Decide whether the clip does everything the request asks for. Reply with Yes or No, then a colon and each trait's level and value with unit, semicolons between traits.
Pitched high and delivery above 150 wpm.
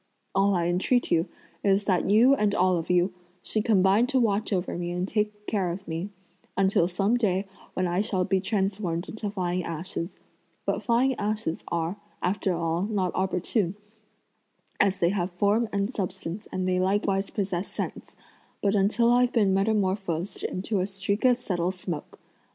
Yes: high, 195 Hz; average, 170 wpm